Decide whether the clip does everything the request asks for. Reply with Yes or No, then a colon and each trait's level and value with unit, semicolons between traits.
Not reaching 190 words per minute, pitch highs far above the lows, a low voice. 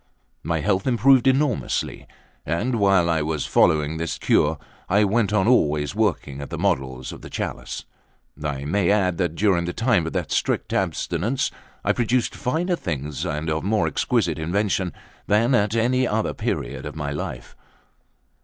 Yes: average, 165 wpm; wide, 6.6 semitones; very low, 95 Hz